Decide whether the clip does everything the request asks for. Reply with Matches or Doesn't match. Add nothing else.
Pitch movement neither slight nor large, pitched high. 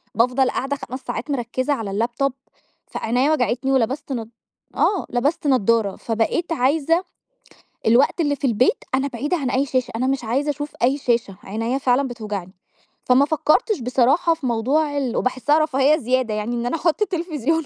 Matches